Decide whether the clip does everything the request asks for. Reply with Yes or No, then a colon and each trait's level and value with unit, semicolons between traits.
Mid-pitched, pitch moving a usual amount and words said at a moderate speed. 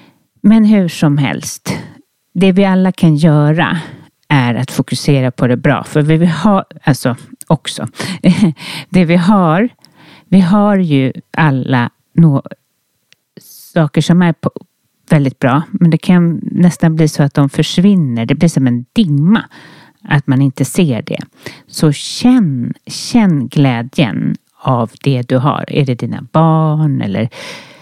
Yes: medium, 155 Hz; average, 4.5 semitones; average, 140 wpm